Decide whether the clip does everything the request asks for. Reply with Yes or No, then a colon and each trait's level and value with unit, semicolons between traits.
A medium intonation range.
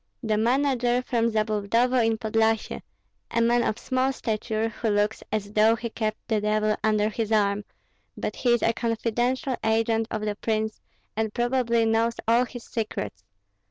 No: narrow, 1.8 semitones